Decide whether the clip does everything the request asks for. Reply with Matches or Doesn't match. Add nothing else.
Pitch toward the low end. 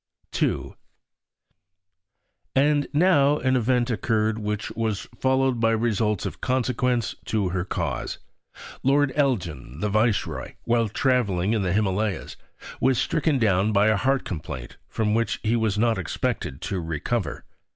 Matches